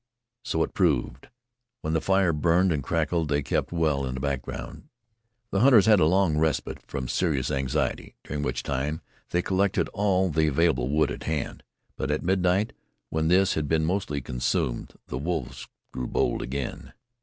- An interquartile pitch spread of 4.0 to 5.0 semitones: Yes, average, 4.6 semitones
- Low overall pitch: Yes, very low, 80 Hz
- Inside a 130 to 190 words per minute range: Yes, average, 170 wpm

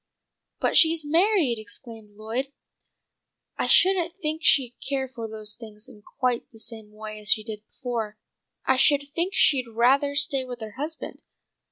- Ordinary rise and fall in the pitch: Yes, average, 4.8 semitones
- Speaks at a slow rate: No, average, 160 wpm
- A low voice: No, very high, 250 Hz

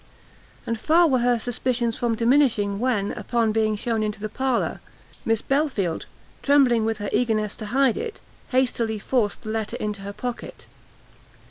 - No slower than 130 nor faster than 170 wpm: Yes, average, 155 wpm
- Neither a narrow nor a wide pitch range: Yes, average, 3.0 semitones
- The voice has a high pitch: Yes, high, 230 Hz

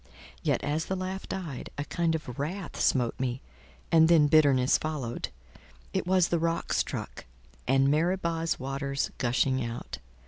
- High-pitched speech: No, medium, 150 Hz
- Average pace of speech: Yes, average, 145 wpm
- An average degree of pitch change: Yes, average, 4.0 semitones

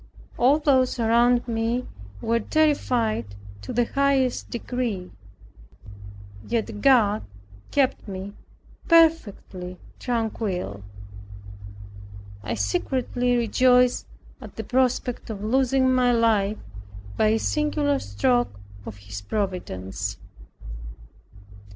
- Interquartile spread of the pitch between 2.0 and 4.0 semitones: No, average, 4.5 semitones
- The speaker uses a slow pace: Yes, slow, 90 wpm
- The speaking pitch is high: Yes, high, 230 Hz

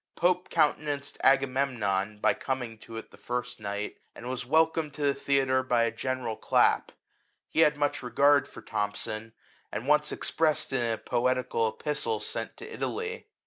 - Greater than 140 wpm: Yes, average, 170 wpm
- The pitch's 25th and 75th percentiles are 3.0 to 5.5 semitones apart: Yes, average, 4.3 semitones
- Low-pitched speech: Yes, low, 130 Hz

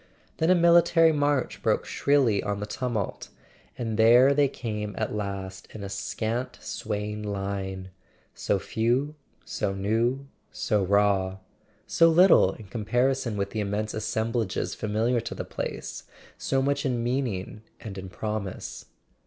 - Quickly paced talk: No, average, 140 wpm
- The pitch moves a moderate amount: Yes, average, 4.3 semitones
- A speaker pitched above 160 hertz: No, low, 110 Hz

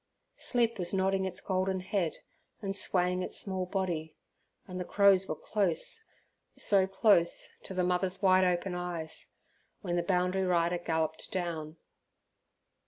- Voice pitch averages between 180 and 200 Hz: Yes, medium, 185 Hz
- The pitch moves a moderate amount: No, narrow, 1.7 semitones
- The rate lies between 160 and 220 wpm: No, average, 140 wpm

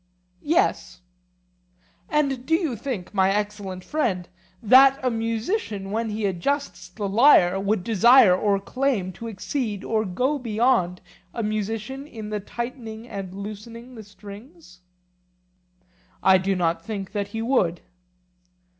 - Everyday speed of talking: No, slow, 130 wpm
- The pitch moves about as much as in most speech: Yes, average, 4.3 semitones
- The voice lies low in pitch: No, high, 215 Hz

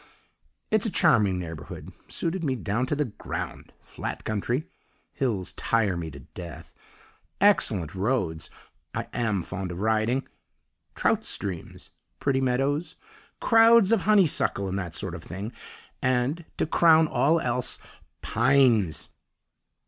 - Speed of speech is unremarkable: No, slow, 125 wpm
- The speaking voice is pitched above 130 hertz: No, low, 120 Hz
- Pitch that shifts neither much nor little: No, wide, 8.0 semitones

